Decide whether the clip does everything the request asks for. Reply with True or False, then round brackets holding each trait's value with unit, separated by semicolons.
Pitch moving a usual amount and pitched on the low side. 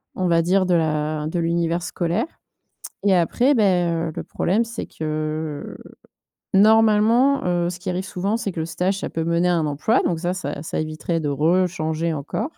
False (3.3 semitones; 175 Hz)